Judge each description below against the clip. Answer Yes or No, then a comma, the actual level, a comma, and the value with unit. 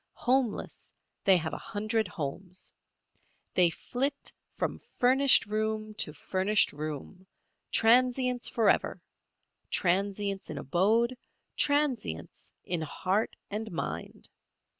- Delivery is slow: Yes, slow, 95 wpm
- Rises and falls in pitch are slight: No, average, 4.9 semitones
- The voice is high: Yes, high, 210 Hz